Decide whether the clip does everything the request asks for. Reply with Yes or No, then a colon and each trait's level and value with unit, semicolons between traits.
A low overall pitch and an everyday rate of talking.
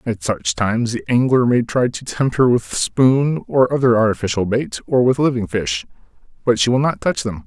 No: low, 115 Hz; fast, 210 wpm